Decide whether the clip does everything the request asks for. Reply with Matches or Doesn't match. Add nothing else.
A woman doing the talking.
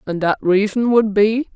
Matches